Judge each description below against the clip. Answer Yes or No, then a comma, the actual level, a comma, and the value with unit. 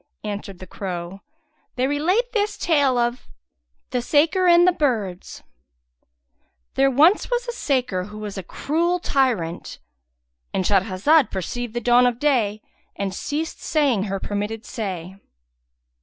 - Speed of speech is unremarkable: No, slow, 130 wpm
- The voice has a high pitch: Yes, high, 240 Hz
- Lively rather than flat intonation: Yes, wide, 7.3 semitones